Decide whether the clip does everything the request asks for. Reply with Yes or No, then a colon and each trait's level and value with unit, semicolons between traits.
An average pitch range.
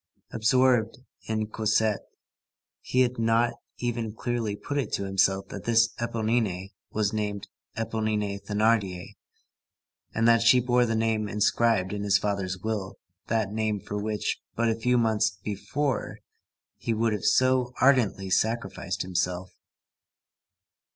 No: narrow, 2.3 semitones